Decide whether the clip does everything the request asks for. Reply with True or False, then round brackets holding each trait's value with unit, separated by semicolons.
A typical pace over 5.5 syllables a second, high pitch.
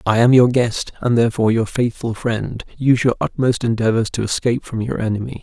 False (5.9 syllables/s; 115 Hz)